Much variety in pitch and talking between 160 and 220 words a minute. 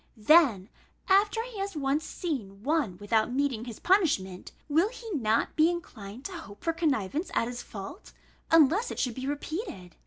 Yes: wide, 7.9 semitones; average, 165 wpm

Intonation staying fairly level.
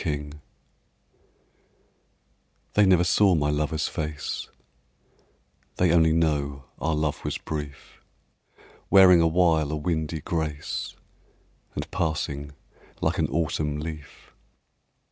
Yes: narrow, 2.0 semitones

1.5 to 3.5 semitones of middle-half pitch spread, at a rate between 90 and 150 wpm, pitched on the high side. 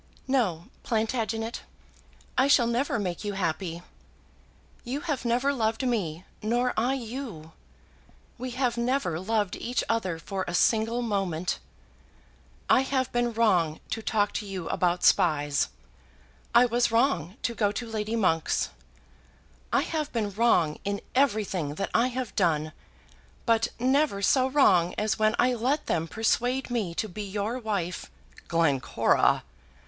No: average, 5.0 semitones; average, 140 wpm; high, 220 Hz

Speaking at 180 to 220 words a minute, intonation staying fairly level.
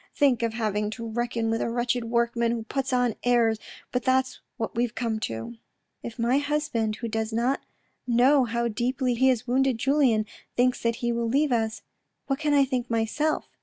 Yes: average, 195 wpm; narrow, 2.3 semitones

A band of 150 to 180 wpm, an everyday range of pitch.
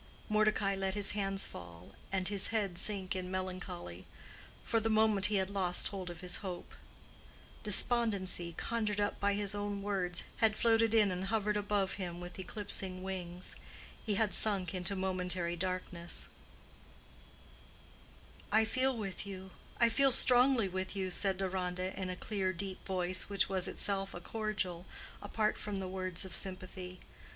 No: average, 155 wpm; narrow, 2.2 semitones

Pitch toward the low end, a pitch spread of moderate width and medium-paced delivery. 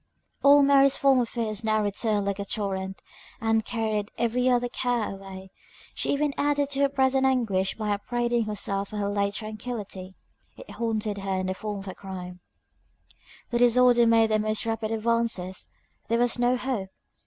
No: high, 220 Hz; average, 3.4 semitones; average, 170 wpm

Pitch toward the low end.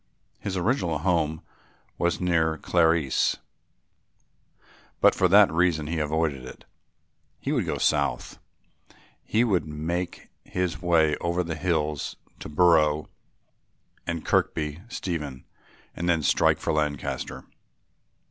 Yes: very low, 80 Hz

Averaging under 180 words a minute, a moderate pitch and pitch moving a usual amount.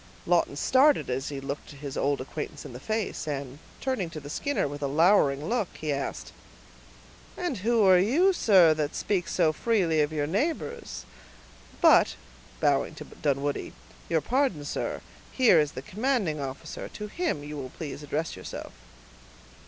No: average, 160 wpm; medium, 155 Hz; wide, 7.2 semitones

